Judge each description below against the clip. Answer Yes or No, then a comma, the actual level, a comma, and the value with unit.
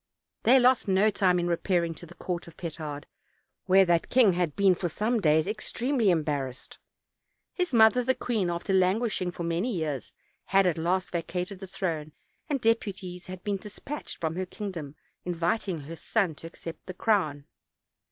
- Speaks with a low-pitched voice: No, medium, 180 Hz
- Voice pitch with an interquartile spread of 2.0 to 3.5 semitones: No, average, 3.9 semitones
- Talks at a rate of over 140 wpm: Yes, average, 170 wpm